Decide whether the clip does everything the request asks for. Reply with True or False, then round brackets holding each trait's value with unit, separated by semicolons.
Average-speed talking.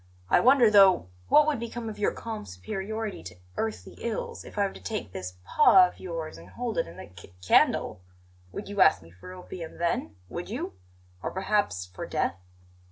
True (195 wpm)